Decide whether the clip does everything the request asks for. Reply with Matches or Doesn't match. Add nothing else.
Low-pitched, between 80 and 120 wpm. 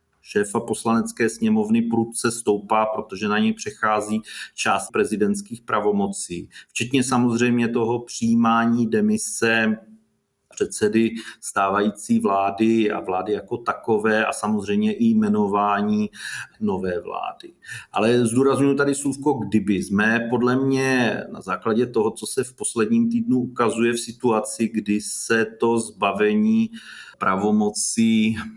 Matches